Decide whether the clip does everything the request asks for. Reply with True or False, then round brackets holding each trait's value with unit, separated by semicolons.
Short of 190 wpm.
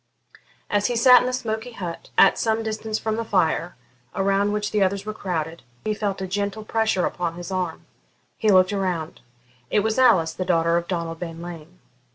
False (195 wpm)